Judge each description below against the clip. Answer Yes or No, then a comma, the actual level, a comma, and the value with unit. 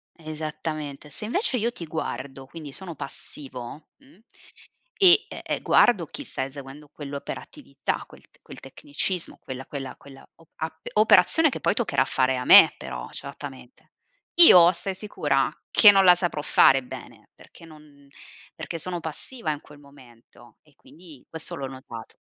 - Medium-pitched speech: Yes, medium, 150 Hz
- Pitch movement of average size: Yes, average, 4.7 semitones